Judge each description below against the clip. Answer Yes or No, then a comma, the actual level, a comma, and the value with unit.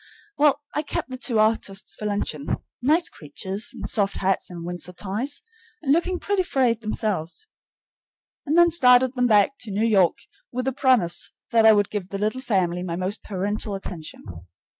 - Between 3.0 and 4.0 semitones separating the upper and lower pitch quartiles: No, average, 5.2 semitones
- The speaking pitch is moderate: No, high, 215 Hz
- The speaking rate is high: No, average, 175 wpm